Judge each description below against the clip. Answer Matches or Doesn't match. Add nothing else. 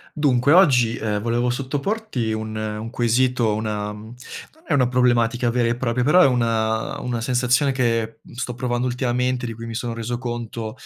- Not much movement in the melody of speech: Matches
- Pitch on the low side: Matches